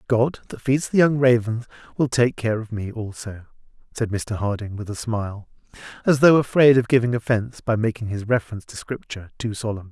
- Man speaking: Yes, male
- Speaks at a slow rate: No, average, 195 wpm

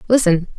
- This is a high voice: Yes, high, 200 Hz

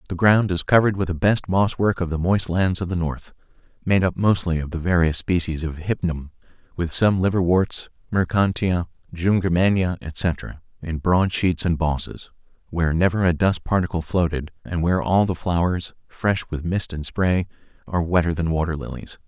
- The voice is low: Yes, very low, 90 Hz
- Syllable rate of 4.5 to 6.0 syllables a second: Yes, 5.0 syllables/s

